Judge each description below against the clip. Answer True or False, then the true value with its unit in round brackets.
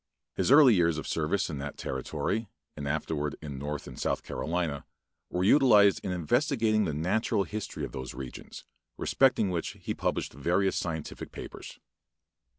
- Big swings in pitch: True (6.3 semitones)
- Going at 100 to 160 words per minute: True (155 wpm)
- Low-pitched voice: True (90 Hz)